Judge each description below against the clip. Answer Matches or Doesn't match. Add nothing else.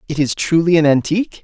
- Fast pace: Matches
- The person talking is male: Matches